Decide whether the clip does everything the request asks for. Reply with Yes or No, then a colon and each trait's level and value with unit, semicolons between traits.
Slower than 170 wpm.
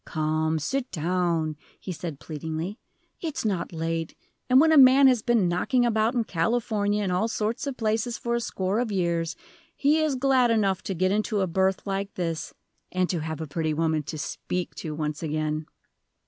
No: average, 190 wpm